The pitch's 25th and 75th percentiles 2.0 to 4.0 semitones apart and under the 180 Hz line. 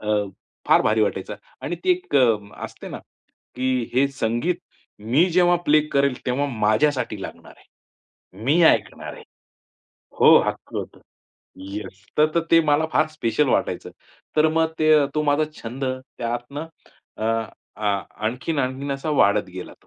No: average, 4.9 semitones; low, 135 Hz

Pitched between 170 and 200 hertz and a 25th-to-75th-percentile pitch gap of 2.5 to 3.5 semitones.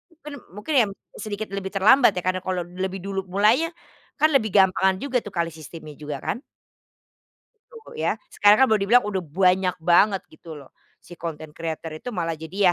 No: high, 190 Hz; average, 4.0 semitones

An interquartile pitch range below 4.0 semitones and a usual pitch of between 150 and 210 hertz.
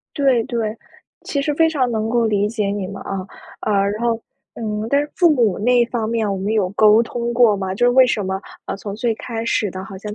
No: average, 2.8 semitones; high, 225 Hz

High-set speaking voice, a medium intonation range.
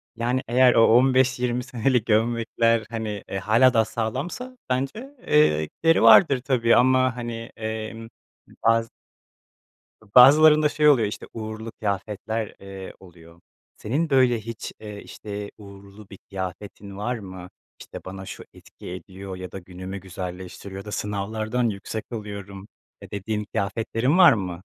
No: low, 110 Hz; average, 4.0 semitones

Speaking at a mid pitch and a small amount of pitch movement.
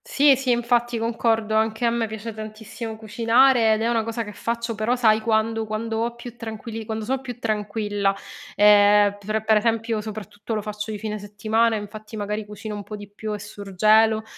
No: high, 220 Hz; narrow, 1.5 semitones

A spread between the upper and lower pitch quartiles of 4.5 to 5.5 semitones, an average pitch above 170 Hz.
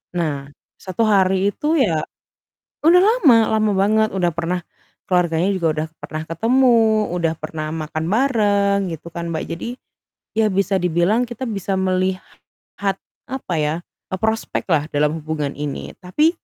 Yes: average, 5.0 semitones; medium, 185 Hz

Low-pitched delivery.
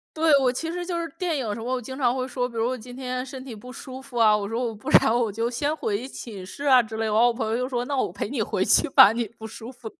No: high, 245 Hz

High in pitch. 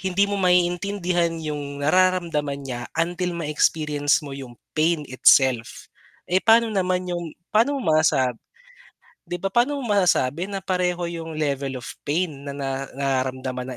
No: medium, 165 Hz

